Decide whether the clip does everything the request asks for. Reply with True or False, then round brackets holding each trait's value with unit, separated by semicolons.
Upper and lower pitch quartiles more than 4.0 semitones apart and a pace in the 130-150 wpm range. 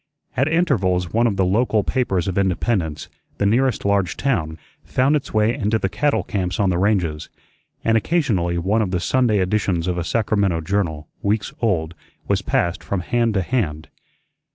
False (4.5 semitones; 175 wpm)